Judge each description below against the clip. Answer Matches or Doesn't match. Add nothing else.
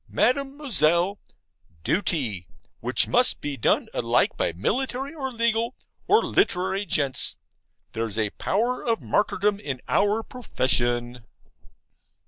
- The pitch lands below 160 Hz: Doesn't match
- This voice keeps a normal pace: Doesn't match